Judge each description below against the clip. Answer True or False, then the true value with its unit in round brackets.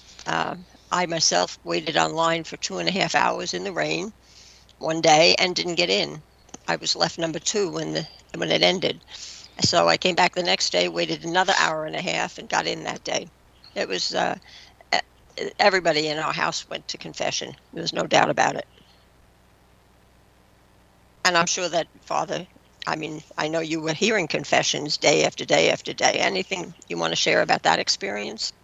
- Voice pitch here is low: False (165 Hz)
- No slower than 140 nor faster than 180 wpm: False (190 wpm)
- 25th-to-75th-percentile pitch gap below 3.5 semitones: True (2.5 semitones)